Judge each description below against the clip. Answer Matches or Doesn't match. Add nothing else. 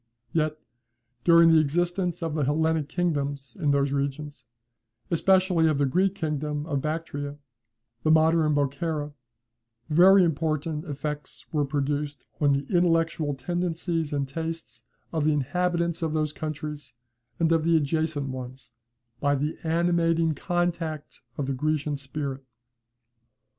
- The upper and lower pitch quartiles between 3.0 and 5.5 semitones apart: Doesn't match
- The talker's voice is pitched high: Doesn't match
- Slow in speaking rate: Matches